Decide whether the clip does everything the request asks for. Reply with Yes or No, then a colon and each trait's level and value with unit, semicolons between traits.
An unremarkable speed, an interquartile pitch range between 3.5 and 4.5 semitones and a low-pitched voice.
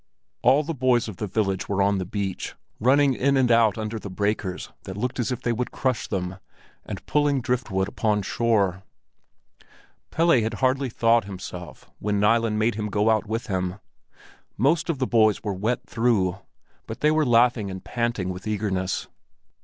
Yes: average, 175 wpm; average, 3.8 semitones; low, 110 Hz